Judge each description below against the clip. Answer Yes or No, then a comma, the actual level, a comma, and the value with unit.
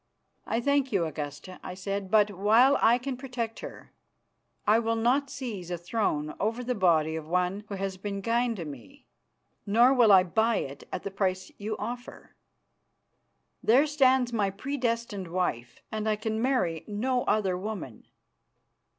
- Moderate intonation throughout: Yes, average, 4.6 semitones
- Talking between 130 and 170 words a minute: Yes, average, 160 wpm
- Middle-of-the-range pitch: No, high, 210 Hz